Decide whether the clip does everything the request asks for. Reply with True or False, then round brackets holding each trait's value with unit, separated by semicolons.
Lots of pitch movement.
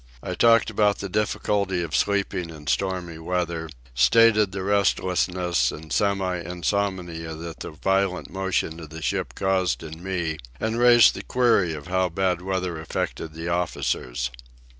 False (3.2 semitones)